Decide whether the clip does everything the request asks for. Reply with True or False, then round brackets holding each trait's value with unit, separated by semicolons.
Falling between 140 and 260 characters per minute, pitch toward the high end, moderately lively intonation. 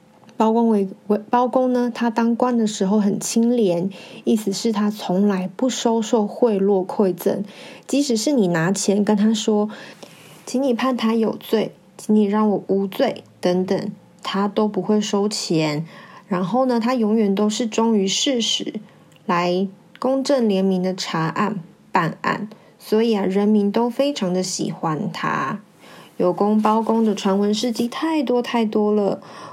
True (215 characters per minute; 210 Hz; 3.1 semitones)